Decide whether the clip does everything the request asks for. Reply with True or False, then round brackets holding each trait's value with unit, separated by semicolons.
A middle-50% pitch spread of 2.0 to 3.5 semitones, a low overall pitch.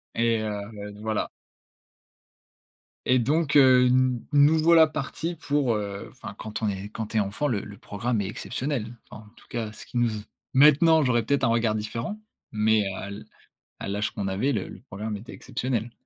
False (4.4 semitones; 115 Hz)